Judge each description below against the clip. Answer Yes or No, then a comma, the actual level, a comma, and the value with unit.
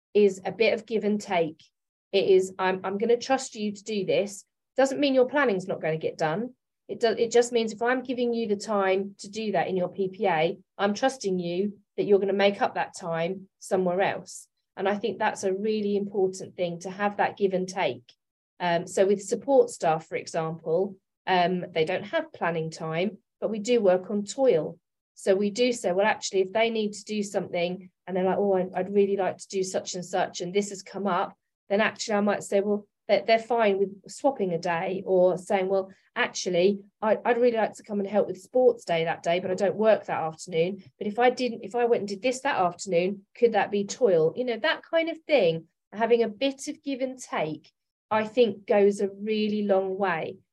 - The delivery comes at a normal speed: No, fast, 225 wpm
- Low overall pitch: No, high, 200 Hz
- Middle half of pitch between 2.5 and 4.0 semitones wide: Yes, average, 3.4 semitones